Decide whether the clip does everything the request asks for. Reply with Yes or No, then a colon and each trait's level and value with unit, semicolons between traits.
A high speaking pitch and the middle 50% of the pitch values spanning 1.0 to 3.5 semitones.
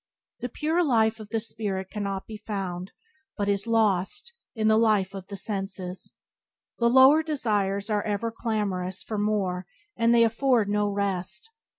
Yes: high, 210 Hz; average, 2.8 semitones